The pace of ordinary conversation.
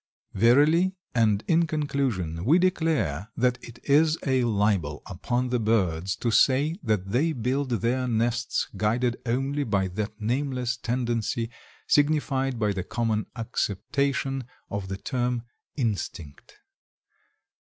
No: slow, 120 wpm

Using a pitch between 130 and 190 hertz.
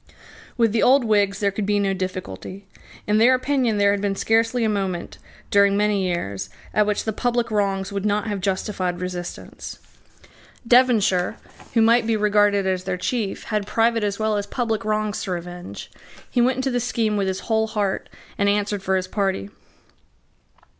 No: high, 205 Hz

